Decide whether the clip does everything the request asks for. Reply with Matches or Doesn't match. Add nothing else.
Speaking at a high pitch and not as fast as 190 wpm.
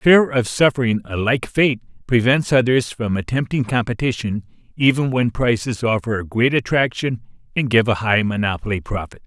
Doesn't match